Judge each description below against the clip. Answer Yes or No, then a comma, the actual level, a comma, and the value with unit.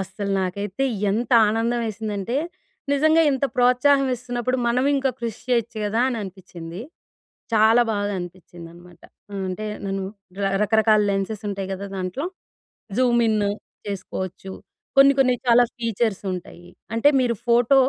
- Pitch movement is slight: No, average, 4.0 semitones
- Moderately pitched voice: No, high, 220 Hz